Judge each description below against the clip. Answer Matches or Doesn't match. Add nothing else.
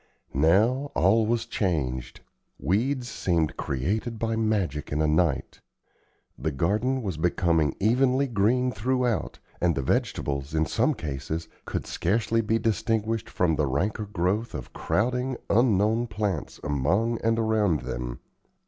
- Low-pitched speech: Matches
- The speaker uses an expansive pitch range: Matches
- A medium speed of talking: Doesn't match